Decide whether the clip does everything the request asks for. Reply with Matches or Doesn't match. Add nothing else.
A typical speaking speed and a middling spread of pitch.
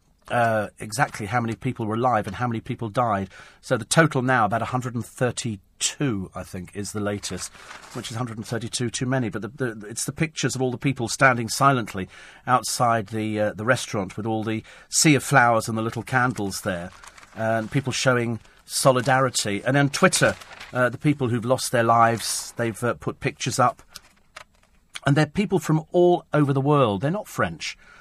Doesn't match